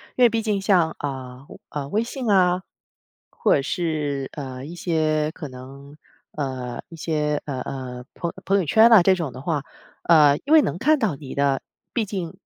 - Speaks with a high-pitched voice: No, medium, 155 Hz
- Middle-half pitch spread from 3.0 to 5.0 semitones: No, wide, 5.4 semitones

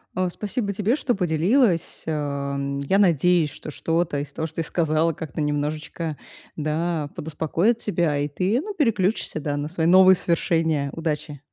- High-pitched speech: No, medium, 160 Hz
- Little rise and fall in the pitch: No, average, 3.8 semitones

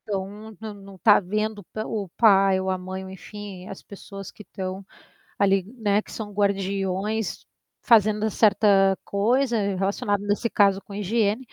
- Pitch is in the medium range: No, high, 200 Hz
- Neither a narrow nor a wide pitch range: No, narrow, 1.8 semitones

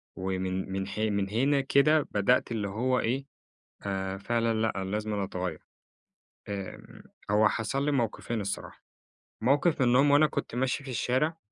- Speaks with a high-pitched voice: No, low, 110 Hz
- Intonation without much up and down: No, average, 5.2 semitones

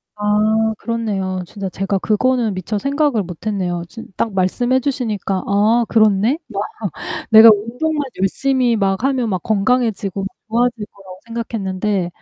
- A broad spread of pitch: No, average, 3.4 semitones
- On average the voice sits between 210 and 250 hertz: Yes, high, 215 Hz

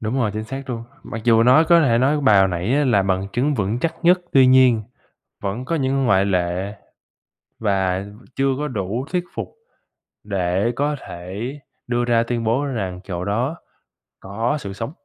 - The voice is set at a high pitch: No, low, 115 Hz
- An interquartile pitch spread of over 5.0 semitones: Yes, wide, 5.4 semitones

